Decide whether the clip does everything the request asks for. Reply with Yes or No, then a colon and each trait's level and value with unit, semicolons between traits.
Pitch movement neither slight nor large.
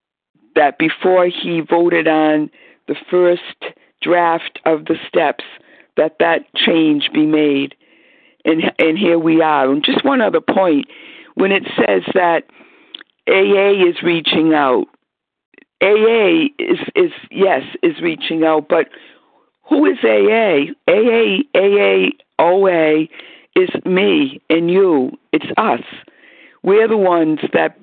No: wide, 6.6 semitones